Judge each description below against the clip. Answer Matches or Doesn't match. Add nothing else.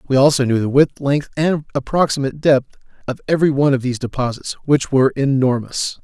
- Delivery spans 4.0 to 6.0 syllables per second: Doesn't match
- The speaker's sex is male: Matches